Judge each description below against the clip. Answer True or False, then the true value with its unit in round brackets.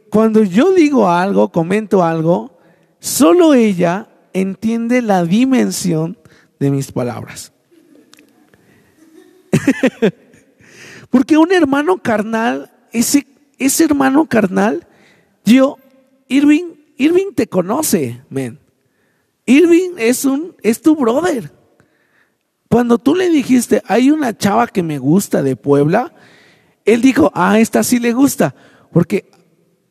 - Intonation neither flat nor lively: False (7.2 semitones)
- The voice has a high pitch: True (230 Hz)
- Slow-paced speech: True (110 wpm)